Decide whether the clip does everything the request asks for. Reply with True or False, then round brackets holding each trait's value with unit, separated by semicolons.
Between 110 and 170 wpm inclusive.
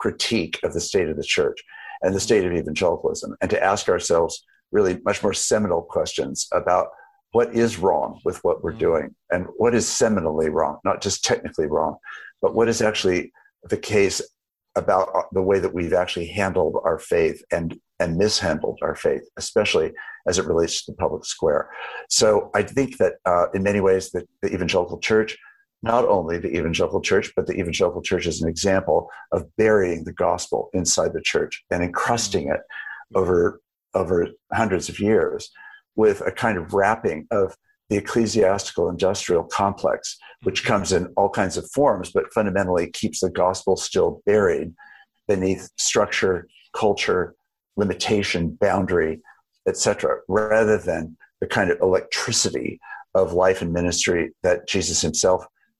True (160 wpm)